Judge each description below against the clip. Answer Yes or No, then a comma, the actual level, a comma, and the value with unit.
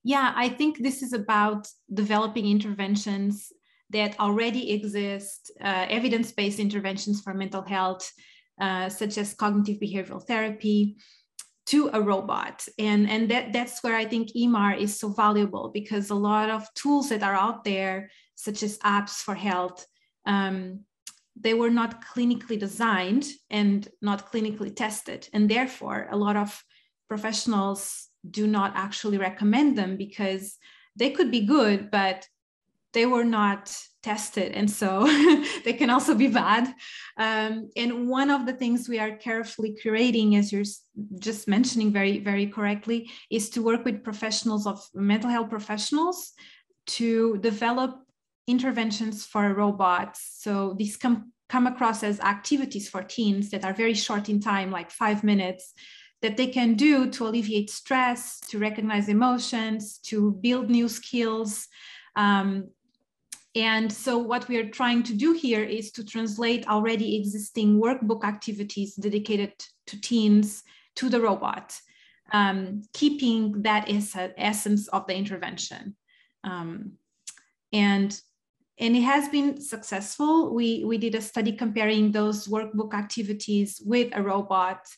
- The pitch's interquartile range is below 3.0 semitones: Yes, narrow, 2.5 semitones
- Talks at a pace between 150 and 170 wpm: No, average, 140 wpm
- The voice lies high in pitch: Yes, high, 215 Hz